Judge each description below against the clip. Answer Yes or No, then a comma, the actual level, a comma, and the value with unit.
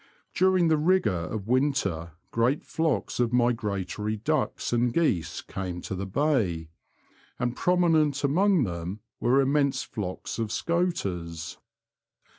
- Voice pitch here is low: Yes, low, 120 Hz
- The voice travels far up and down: Yes, wide, 7.9 semitones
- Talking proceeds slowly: Yes, slow, 120 wpm